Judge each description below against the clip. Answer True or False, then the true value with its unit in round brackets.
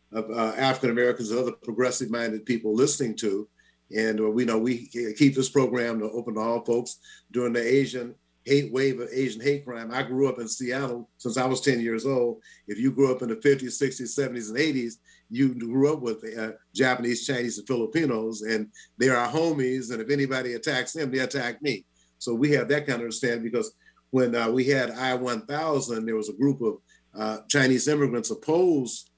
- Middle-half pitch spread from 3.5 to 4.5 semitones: False (2.7 semitones)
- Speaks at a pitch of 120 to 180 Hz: True (125 Hz)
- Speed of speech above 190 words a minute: True (200 wpm)